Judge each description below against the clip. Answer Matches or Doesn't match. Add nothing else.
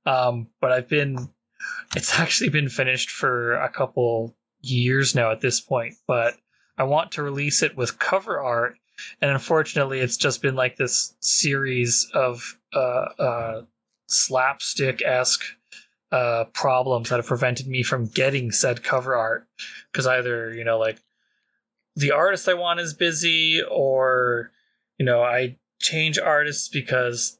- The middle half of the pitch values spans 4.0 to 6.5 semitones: Doesn't match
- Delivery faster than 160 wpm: Doesn't match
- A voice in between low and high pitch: Doesn't match